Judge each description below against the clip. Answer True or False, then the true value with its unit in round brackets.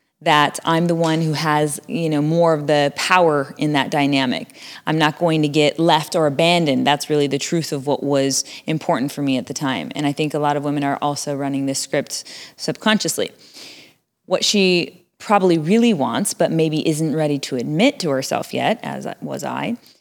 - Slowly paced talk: False (200 wpm)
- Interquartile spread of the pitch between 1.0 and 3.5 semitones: True (2.8 semitones)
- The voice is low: False (150 Hz)